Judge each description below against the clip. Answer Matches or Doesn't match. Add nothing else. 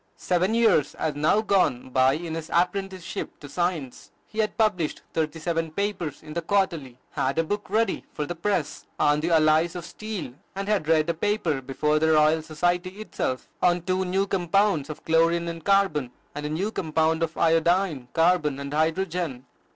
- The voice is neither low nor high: Matches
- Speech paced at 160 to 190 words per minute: Matches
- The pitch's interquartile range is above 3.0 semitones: Matches